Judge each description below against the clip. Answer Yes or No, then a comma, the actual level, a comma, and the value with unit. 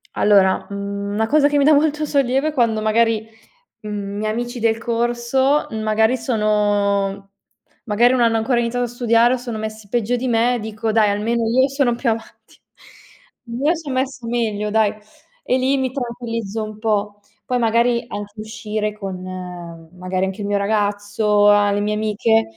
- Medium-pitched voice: No, high, 225 Hz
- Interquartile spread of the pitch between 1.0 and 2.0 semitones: No, average, 2.7 semitones